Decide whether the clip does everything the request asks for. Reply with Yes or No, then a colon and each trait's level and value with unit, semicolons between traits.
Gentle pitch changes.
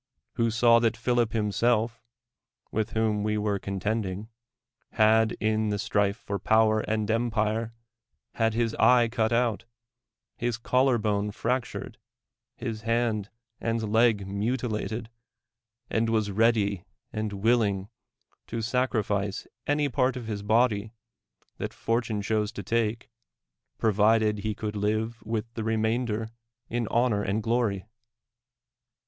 Yes: narrow, 1.8 semitones